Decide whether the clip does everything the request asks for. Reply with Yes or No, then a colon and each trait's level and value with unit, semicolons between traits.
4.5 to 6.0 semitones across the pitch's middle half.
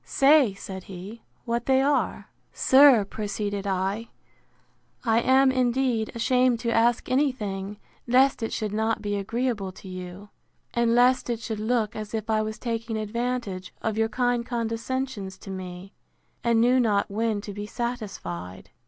No: average, 3.3 semitones